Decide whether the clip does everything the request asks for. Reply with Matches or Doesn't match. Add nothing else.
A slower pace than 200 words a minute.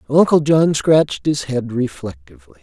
Matches